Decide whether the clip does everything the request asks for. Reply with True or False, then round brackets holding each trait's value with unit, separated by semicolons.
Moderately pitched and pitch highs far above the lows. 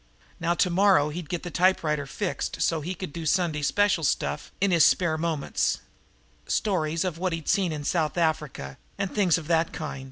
False (165 Hz; 3.0 semitones)